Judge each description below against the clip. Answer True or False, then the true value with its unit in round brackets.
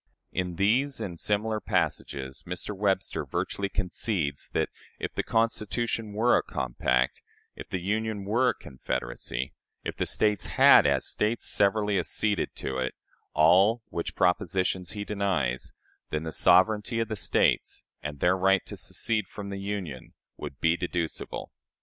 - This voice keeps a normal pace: True (150 wpm)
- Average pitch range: True (4.6 semitones)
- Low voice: True (95 Hz)